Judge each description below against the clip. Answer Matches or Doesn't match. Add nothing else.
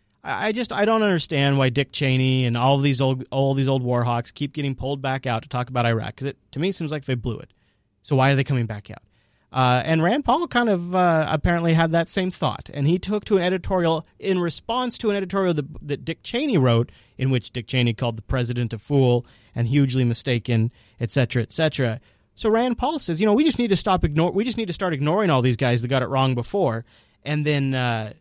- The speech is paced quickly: Matches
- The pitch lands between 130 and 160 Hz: Matches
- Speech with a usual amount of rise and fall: Doesn't match